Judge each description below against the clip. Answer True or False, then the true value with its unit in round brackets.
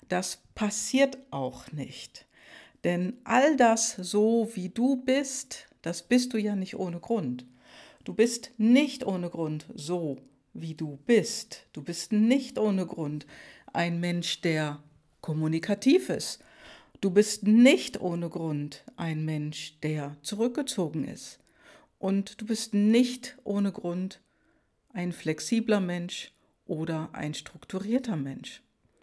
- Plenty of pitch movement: True (6.3 semitones)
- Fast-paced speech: False (125 wpm)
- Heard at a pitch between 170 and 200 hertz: True (185 Hz)